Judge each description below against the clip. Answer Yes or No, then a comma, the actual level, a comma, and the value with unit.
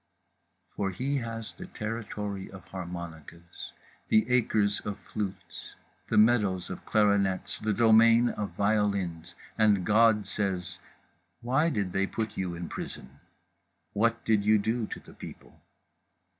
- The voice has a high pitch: No, low, 105 Hz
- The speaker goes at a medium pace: No, slow, 130 wpm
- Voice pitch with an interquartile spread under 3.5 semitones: Yes, average, 3.0 semitones